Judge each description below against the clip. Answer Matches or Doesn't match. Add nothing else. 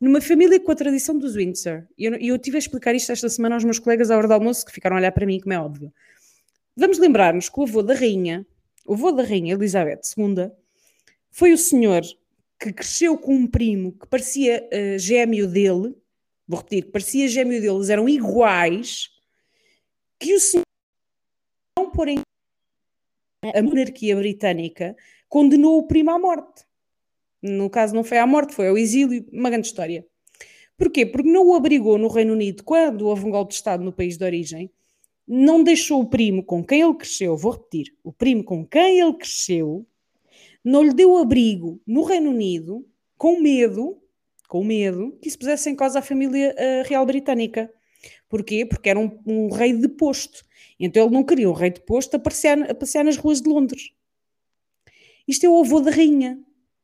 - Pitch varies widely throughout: Matches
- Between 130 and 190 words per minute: Matches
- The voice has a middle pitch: Doesn't match